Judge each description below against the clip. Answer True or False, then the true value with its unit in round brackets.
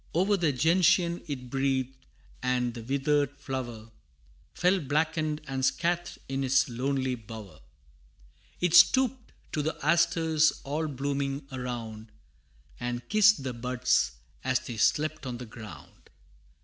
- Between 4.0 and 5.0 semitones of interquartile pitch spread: True (4.3 semitones)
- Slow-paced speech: True (125 wpm)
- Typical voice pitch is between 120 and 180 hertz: True (135 Hz)